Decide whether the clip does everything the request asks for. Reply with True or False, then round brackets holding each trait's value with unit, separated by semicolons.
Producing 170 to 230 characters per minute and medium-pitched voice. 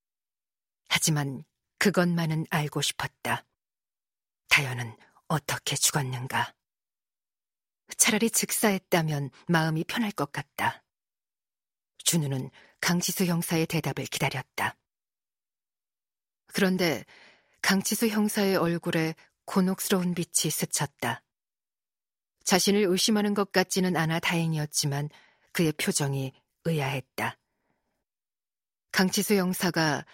True (220 characters per minute; 170 Hz)